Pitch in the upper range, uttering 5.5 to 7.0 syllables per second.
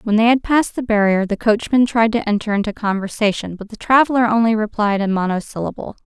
Yes: high, 220 Hz; 6.1 syllables/s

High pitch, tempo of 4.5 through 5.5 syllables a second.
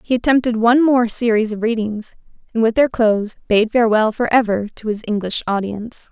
No: high, 225 Hz; 5.7 syllables/s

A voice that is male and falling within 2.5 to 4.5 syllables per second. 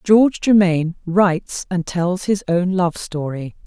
No: female; 4.2 syllables/s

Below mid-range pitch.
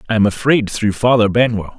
Yes: low, 110 Hz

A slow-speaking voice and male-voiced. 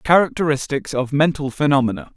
Yes: slow, 110 wpm; male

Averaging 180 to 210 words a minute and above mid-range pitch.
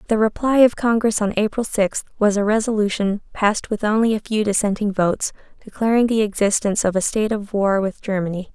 Yes: average, 190 wpm; high, 210 Hz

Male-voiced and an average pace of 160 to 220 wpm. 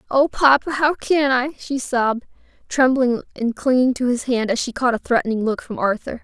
No: female; average, 200 wpm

